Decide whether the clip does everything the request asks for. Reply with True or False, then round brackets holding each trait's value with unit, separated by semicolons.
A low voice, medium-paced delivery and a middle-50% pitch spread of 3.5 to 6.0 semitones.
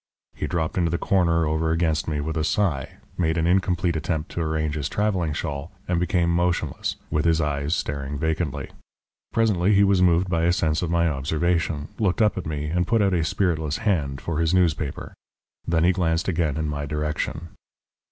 False (80 Hz; 190 wpm; 2.6 semitones)